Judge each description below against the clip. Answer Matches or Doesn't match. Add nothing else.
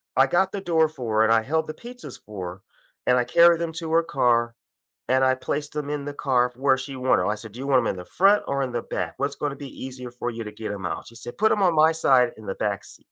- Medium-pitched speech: Doesn't match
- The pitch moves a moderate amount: Matches